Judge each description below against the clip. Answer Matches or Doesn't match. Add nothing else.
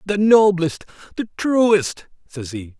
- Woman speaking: Doesn't match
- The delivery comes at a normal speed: Doesn't match